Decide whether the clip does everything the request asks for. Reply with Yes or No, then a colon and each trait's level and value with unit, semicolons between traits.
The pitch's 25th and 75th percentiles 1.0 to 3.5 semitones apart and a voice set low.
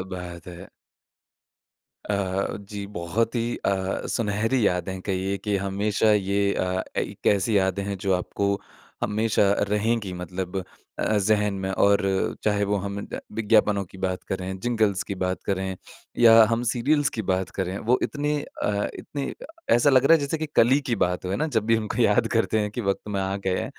Yes: average, 2.8 semitones; low, 100 Hz